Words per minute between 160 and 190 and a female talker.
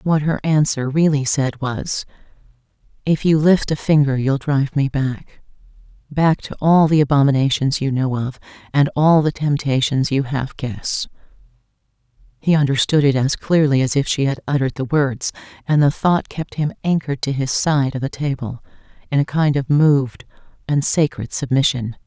Yes: average, 170 wpm; female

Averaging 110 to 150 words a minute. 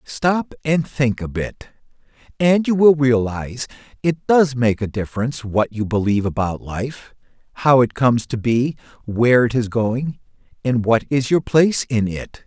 No: average, 170 wpm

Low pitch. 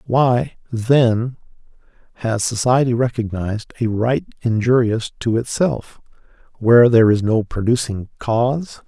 Yes: low, 120 Hz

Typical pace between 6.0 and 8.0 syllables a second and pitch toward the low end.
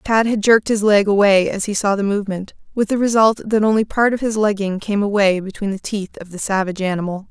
No: 6.1 syllables/s; high, 205 Hz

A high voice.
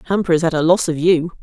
No: medium, 170 Hz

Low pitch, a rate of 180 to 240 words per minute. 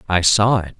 Yes: very low, 95 Hz; fast, 225 wpm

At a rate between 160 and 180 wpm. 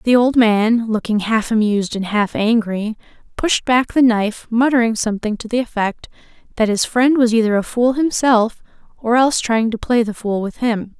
No: average, 190 wpm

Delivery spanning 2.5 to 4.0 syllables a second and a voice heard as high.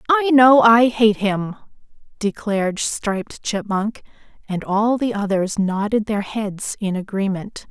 Yes: 3.9 syllables/s; high, 210 Hz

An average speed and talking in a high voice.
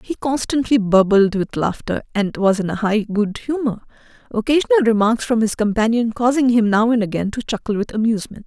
Yes: average, 185 wpm; high, 225 Hz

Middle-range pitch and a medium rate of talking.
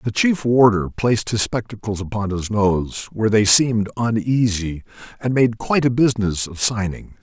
No: low, 110 Hz; average, 165 wpm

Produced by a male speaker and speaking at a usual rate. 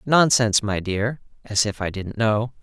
Yes: male; average, 185 wpm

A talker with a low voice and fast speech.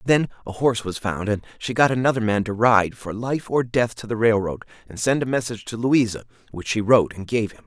Yes: low, 115 Hz; fast, 245 wpm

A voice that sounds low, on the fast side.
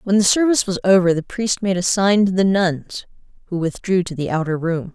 No: medium, 185 Hz; fast, 230 wpm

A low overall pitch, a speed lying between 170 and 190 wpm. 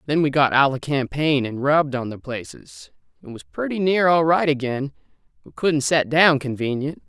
No: medium, 145 Hz; average, 180 wpm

